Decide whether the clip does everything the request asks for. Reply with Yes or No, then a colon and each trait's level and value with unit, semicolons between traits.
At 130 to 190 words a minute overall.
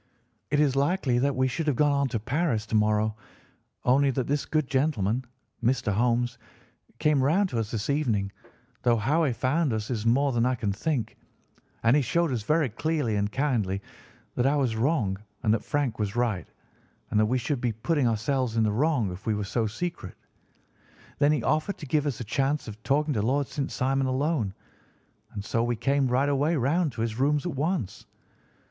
No: average, 200 wpm